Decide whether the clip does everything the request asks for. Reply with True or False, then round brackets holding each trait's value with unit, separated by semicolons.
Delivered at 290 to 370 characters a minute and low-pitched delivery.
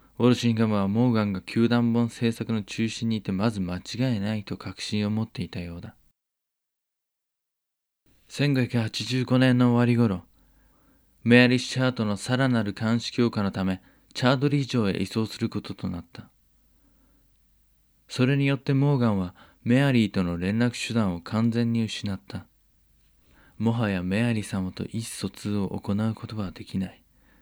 True (300 characters per minute; 110 Hz)